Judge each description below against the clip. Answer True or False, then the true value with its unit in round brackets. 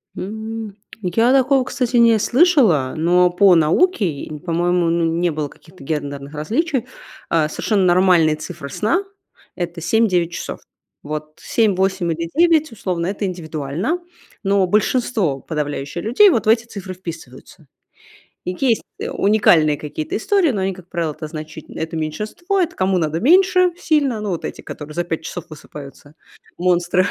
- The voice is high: False (180 Hz)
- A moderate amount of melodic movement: False (6.0 semitones)